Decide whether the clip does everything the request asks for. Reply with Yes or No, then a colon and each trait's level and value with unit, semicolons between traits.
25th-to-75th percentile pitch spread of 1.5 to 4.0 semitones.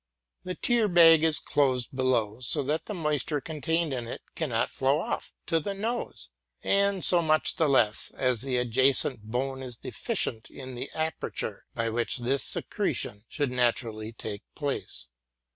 No: average, 5.0 semitones